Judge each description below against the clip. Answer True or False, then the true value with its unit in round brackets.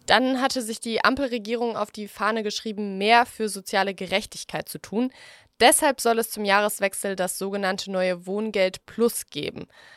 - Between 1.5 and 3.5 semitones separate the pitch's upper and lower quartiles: True (3.1 semitones)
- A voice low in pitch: False (210 Hz)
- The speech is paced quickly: False (155 wpm)